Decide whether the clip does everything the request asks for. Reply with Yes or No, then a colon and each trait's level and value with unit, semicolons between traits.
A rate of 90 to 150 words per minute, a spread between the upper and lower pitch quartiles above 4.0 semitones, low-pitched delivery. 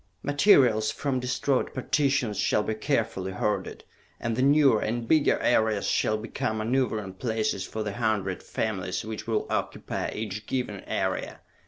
No: average, 145 wpm; average, 3.5 semitones; low, 110 Hz